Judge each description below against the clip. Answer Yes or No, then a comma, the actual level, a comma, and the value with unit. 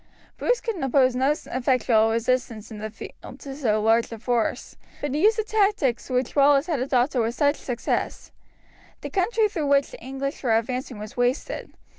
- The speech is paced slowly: No, average, 180 wpm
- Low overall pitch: No, very high, 260 Hz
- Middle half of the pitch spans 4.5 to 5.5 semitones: No, average, 3.8 semitones